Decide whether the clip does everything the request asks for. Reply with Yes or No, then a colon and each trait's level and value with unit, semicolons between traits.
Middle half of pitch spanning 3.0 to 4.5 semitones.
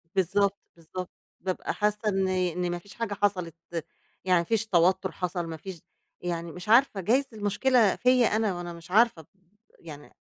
Yes: average, 3.3 semitones